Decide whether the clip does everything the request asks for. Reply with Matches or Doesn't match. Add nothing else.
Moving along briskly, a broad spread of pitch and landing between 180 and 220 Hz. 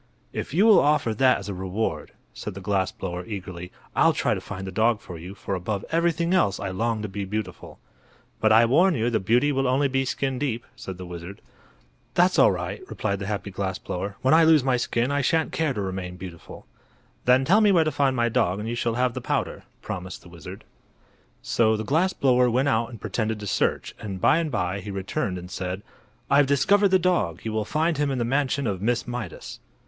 Doesn't match